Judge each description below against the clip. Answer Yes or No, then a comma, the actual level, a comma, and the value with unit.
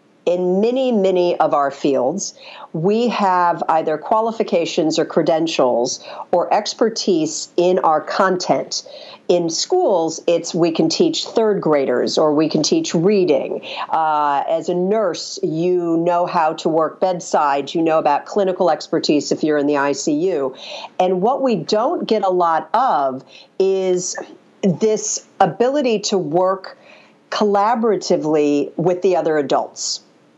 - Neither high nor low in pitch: Yes, medium, 180 Hz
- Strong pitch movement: No, average, 4.4 semitones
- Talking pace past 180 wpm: No, slow, 135 wpm